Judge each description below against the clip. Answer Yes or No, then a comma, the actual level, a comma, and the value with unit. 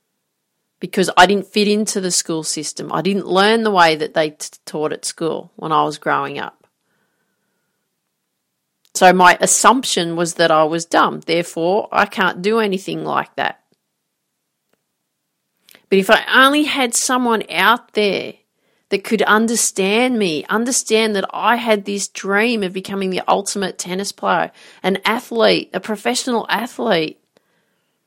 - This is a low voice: No, high, 200 Hz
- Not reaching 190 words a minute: Yes, average, 145 wpm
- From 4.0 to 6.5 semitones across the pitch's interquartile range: No, average, 3.5 semitones